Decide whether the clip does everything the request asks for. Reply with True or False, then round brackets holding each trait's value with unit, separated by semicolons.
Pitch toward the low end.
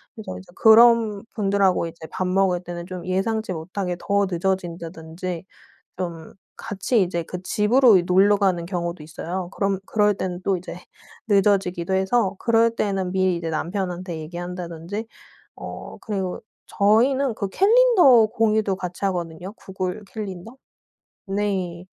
False (190 Hz)